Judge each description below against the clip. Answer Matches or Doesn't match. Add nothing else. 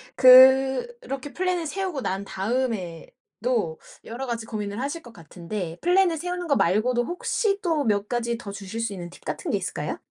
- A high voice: Matches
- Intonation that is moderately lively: Doesn't match